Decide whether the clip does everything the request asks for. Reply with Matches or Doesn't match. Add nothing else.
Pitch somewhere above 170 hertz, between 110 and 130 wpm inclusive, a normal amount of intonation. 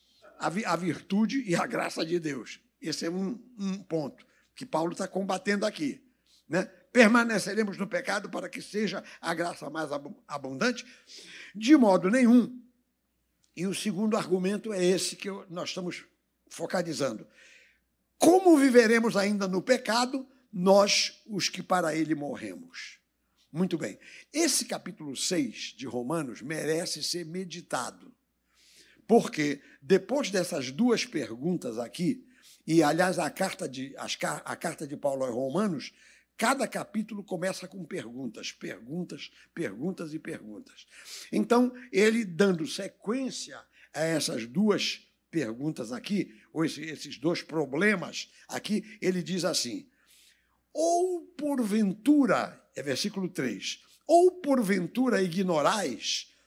Doesn't match